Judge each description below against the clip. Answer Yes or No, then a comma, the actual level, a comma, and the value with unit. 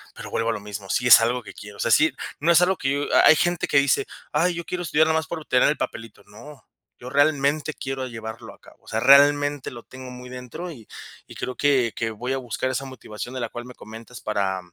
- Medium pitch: No, low, 130 Hz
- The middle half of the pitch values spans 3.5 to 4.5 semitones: Yes, average, 4.1 semitones